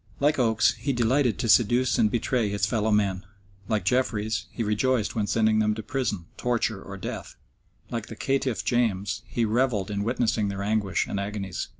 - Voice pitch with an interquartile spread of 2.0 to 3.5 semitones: Yes, average, 2.9 semitones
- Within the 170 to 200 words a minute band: Yes, average, 180 wpm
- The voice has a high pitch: No, low, 110 Hz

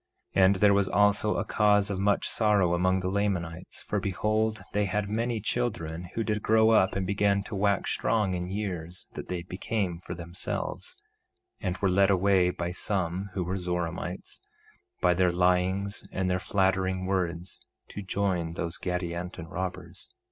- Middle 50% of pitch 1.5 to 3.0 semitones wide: Yes, narrow, 2.4 semitones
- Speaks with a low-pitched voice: Yes, very low, 95 Hz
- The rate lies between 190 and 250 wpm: No, average, 165 wpm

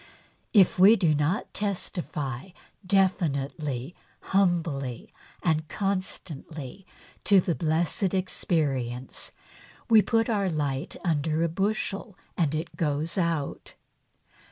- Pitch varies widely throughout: No, average, 4.6 semitones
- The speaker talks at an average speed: No, slow, 100 wpm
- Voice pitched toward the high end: No, medium, 170 Hz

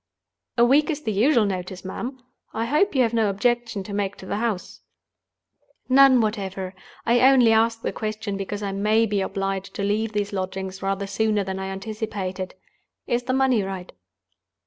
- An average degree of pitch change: Yes, average, 3.4 semitones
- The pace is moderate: Yes, average, 175 wpm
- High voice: Yes, high, 210 Hz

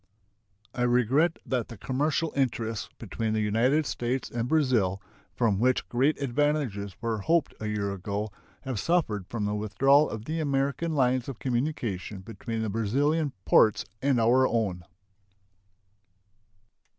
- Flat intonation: No, average, 4.6 semitones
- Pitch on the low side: Yes, low, 120 Hz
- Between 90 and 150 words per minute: Yes, average, 140 wpm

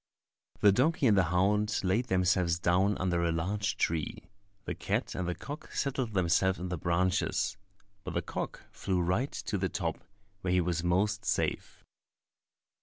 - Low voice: Yes, very low, 95 Hz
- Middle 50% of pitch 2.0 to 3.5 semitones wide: Yes, average, 2.9 semitones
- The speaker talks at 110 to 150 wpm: No, average, 165 wpm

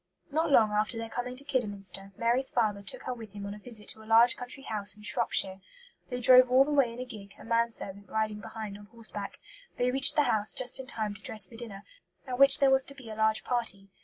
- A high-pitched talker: Yes, high, 225 Hz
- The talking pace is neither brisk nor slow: No, fast, 250 wpm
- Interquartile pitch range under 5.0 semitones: Yes, average, 3.4 semitones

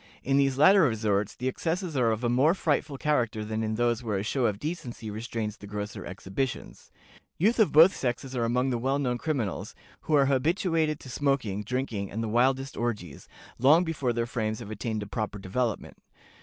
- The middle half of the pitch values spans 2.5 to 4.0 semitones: No, average, 4.4 semitones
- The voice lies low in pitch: Yes, low, 120 Hz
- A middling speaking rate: Yes, average, 195 wpm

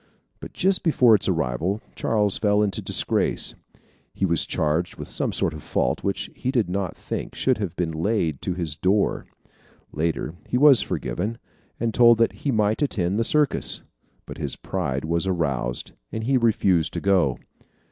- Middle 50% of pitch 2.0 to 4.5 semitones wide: No, wide, 5.5 semitones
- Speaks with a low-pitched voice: Yes, low, 100 Hz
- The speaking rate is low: No, average, 165 wpm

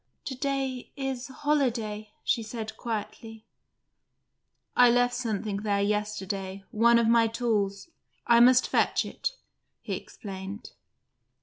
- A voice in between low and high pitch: No, high, 230 Hz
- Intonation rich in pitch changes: No, average, 2.9 semitones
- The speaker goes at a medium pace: No, slow, 115 wpm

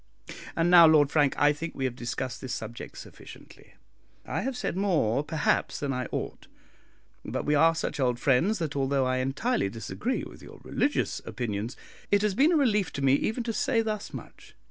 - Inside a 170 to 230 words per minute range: Yes, average, 190 wpm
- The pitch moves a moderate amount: No, wide, 8.0 semitones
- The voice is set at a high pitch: No, medium, 150 Hz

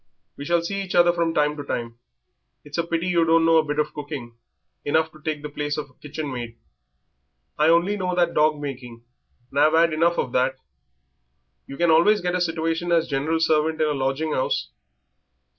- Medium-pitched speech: Yes, medium, 155 Hz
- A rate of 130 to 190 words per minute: No, average, 200 wpm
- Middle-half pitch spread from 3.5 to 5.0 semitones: No, narrow, 2.6 semitones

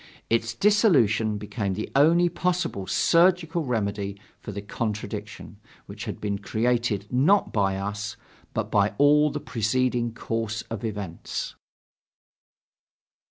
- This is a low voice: Yes, low, 115 Hz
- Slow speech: Yes, slow, 115 wpm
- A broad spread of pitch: Yes, wide, 5.8 semitones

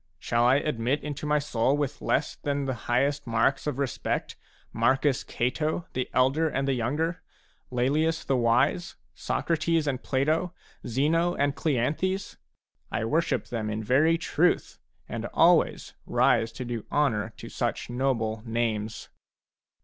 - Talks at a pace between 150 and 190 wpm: No, average, 140 wpm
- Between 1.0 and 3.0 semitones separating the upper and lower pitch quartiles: No, average, 4.2 semitones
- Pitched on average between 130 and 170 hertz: Yes, low, 135 Hz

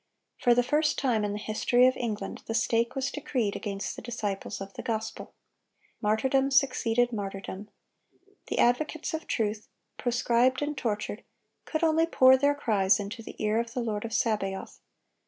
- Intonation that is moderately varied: Yes, average, 3.6 semitones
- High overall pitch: Yes, high, 230 Hz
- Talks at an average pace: Yes, average, 165 wpm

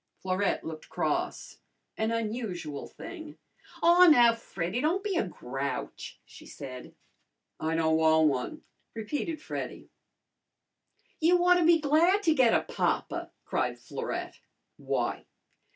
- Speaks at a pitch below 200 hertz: No, high, 230 Hz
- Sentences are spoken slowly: Yes, slow, 125 wpm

